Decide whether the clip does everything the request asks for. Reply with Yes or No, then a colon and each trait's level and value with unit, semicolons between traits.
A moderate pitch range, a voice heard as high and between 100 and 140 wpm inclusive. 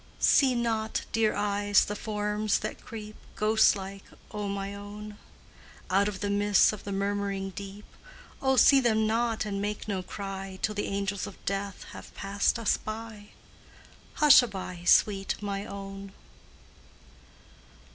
No: narrow, 1.5 semitones; high, 205 Hz; slow, 135 wpm